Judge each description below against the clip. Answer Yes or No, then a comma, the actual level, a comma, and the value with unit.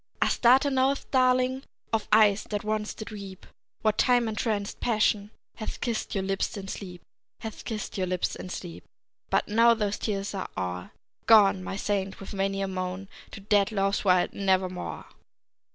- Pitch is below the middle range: No, high, 205 Hz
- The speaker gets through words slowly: No, average, 165 wpm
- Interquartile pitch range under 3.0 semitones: Yes, narrow, 2.4 semitones